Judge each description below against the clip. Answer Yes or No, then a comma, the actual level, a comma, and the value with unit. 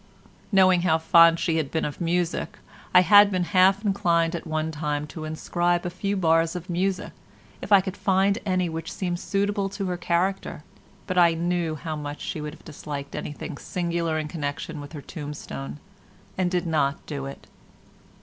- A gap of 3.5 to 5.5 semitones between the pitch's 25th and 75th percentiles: No, average, 2.9 semitones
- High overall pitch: No, medium, 170 Hz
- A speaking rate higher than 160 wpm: Yes, average, 180 wpm